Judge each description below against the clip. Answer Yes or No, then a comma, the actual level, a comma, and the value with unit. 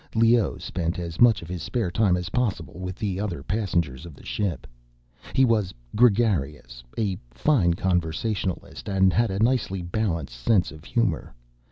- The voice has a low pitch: Yes, very low, 95 Hz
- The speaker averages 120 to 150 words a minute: No, average, 160 wpm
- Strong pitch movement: No, average, 4.6 semitones